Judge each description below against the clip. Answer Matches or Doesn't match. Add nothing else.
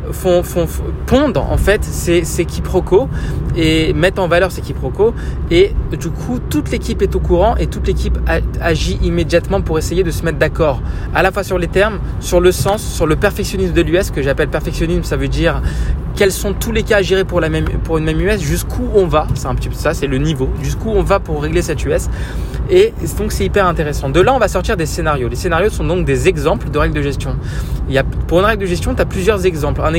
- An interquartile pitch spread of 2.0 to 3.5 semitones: Doesn't match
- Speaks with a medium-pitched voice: Matches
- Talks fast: Matches